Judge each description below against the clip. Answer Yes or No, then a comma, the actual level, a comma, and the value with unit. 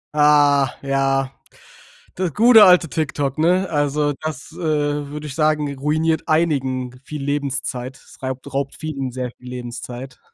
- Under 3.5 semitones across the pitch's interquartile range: Yes, average, 2.7 semitones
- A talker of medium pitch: Yes, medium, 145 Hz